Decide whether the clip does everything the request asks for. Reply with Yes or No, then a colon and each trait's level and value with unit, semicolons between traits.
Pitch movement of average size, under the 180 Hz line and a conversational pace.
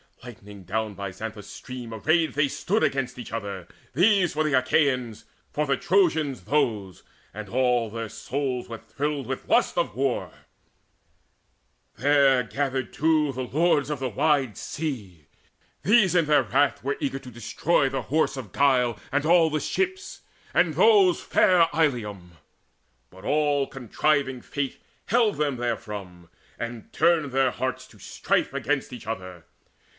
Yes: average, 4.8 semitones; low, 135 Hz; average, 150 wpm